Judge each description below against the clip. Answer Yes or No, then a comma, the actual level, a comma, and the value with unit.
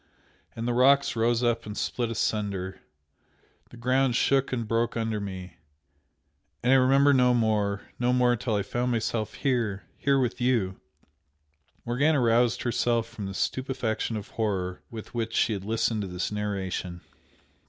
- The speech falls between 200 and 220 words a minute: No, average, 155 wpm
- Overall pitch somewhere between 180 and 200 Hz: No, low, 115 Hz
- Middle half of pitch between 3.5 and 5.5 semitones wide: No, average, 3.0 semitones